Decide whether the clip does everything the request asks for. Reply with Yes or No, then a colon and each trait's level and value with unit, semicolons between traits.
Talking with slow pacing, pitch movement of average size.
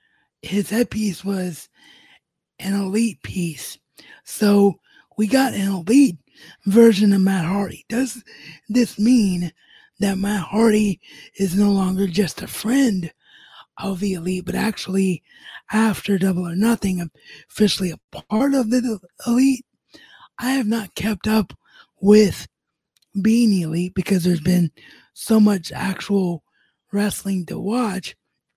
Yes: slow, 125 wpm; average, 3.1 semitones